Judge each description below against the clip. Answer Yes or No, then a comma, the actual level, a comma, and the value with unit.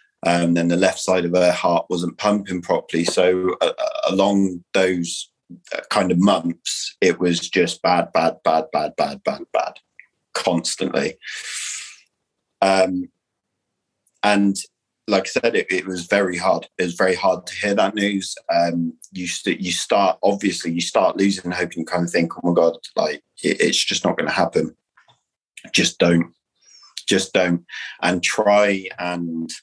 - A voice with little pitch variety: Yes, narrow, 2.2 semitones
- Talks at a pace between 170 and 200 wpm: No, average, 160 wpm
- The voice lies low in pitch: Yes, very low, 90 Hz